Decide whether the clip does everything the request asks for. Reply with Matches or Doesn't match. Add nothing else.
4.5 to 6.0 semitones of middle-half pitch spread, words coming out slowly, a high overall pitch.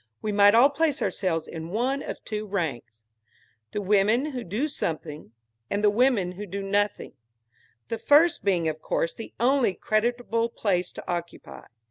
Doesn't match